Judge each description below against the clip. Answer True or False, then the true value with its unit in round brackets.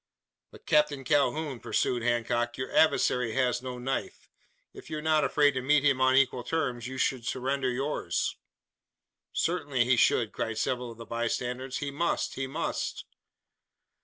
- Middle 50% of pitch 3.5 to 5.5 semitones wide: False (2.8 semitones)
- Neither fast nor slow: True (160 wpm)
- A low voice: True (130 Hz)